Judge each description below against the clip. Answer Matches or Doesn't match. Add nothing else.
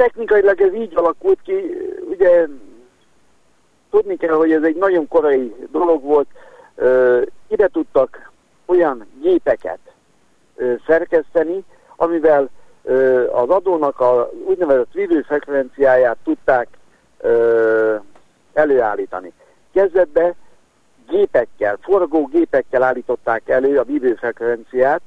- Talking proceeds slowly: Matches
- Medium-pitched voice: Matches